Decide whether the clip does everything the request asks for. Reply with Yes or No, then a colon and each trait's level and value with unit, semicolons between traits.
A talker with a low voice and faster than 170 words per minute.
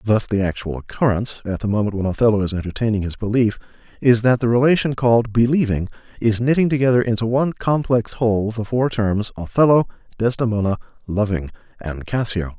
No: low, 110 Hz; average, 160 wpm